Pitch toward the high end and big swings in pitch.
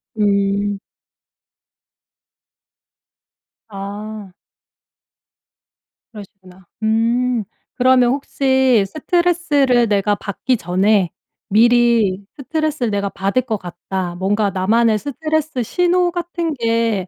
No: high, 225 Hz; average, 4.8 semitones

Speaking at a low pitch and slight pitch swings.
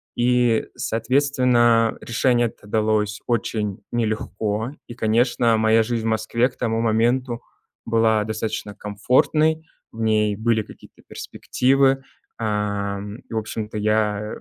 Yes: low, 110 Hz; narrow, 2.0 semitones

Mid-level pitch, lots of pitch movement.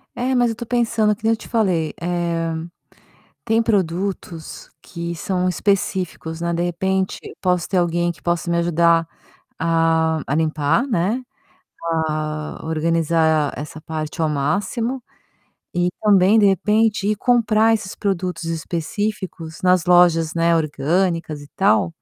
No: medium, 175 Hz; average, 3.8 semitones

